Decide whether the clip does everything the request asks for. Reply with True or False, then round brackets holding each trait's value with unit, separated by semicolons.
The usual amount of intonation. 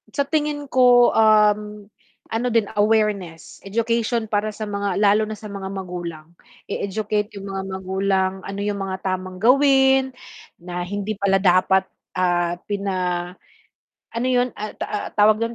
True (3.0 semitones)